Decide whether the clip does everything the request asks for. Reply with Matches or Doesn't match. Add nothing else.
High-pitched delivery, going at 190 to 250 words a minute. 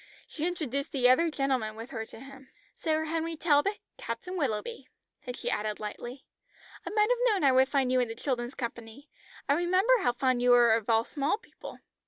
Matches